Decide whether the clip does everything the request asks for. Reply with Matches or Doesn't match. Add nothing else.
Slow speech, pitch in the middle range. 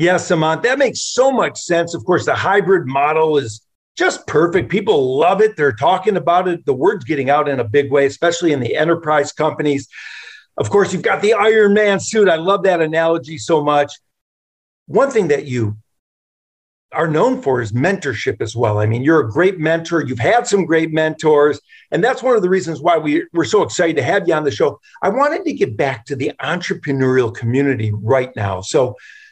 Doesn't match